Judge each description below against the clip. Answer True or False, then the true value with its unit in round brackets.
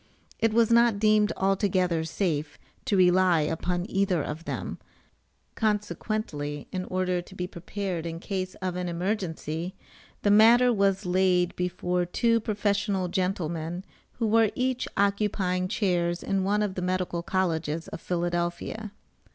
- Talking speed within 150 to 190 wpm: False (135 wpm)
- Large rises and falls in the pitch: False (3.0 semitones)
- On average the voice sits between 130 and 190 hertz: True (185 Hz)